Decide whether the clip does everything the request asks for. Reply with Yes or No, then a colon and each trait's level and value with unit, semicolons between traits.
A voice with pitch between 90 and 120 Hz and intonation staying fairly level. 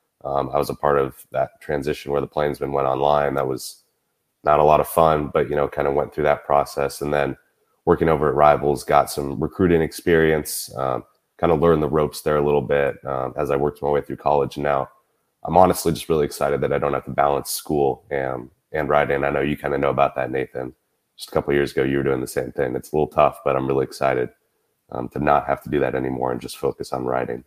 No: very low, 70 Hz; narrow, 1.5 semitones